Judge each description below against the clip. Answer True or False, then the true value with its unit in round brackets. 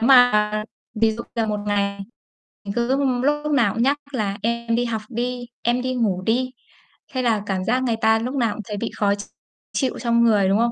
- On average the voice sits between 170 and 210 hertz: False (230 Hz)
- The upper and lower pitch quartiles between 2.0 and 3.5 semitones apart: True (2.8 semitones)